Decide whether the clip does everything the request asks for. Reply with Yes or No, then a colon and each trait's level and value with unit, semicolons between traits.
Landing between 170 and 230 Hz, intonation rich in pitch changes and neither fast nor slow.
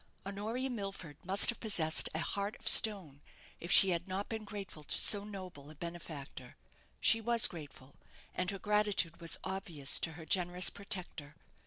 No: medium, 185 Hz; average, 4.1 semitones; average, 165 wpm